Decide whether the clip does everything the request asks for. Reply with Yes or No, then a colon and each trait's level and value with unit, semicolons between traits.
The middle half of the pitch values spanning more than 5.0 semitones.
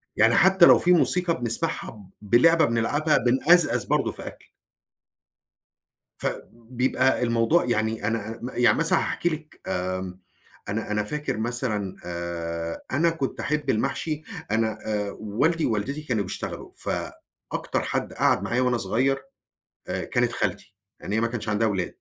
Yes: wide, 5.5 semitones